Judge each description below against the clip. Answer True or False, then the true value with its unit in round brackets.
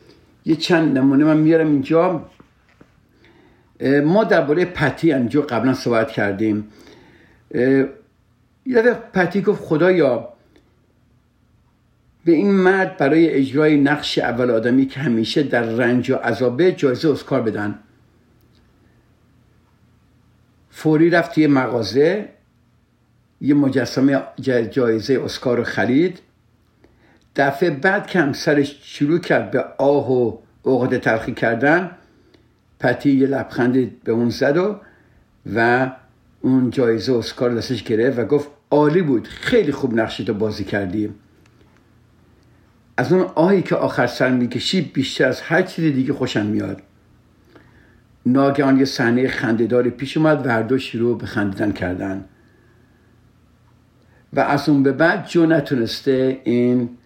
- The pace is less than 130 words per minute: True (120 wpm)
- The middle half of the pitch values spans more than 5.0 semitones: False (3.9 semitones)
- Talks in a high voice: False (125 Hz)